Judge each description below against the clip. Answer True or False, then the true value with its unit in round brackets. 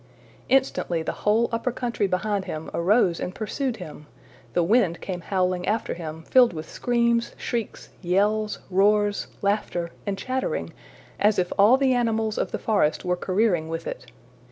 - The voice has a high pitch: True (200 Hz)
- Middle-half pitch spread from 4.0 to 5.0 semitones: True (4.6 semitones)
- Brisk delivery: False (155 wpm)